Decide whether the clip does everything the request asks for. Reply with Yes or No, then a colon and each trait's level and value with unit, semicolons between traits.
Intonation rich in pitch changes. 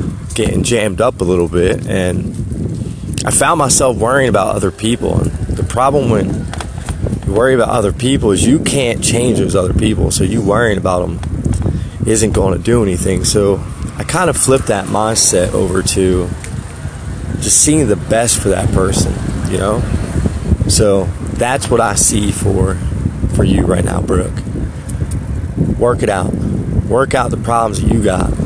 No: average, 3.4 semitones